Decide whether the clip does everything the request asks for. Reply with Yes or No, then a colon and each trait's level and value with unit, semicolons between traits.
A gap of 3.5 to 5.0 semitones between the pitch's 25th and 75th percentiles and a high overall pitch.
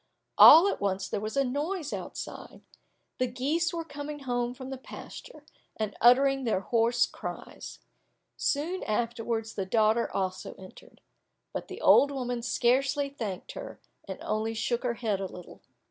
Yes: average, 4.3 semitones; high, 245 Hz